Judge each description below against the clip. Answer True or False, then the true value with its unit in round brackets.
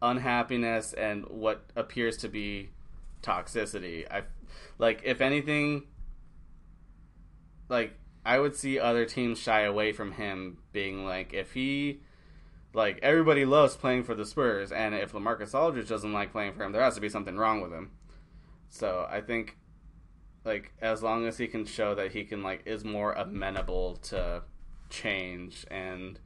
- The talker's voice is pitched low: True (110 Hz)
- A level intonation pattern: False (3.6 semitones)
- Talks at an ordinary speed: True (160 wpm)